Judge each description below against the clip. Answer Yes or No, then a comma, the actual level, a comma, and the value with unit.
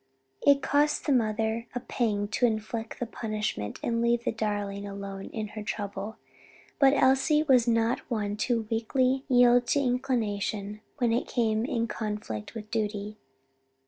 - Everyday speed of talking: Yes, average, 150 wpm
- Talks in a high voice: Yes, high, 225 Hz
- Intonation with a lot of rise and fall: No, average, 2.8 semitones